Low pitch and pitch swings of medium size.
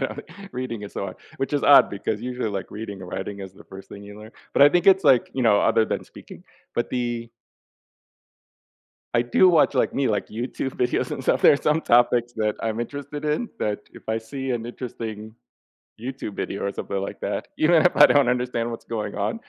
Yes: low, 120 Hz; average, 4.4 semitones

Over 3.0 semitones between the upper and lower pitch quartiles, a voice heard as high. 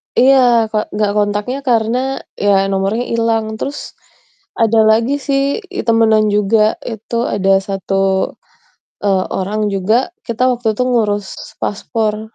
No: average, 2.7 semitones; high, 220 Hz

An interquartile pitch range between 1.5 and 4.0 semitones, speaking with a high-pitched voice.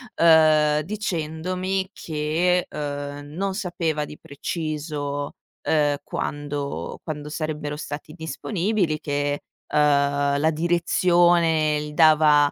No: narrow, 2.6 semitones; medium, 155 Hz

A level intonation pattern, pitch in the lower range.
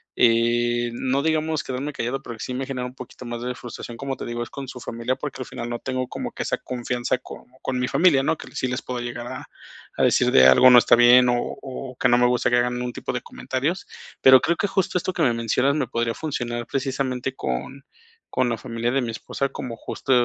Yes: narrow, 2.0 semitones; low, 125 Hz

